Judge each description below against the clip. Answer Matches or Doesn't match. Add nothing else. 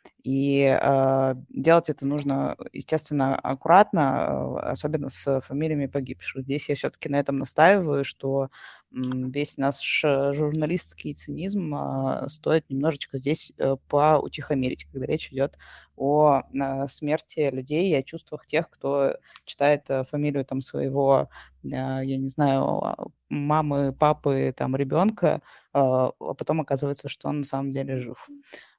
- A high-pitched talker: Doesn't match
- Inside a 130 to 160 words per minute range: Doesn't match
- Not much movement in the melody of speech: Matches